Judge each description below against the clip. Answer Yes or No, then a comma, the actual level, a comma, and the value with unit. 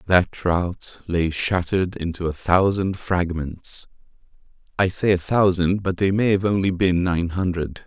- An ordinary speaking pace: Yes, average, 145 wpm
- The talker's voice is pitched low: Yes, very low, 90 Hz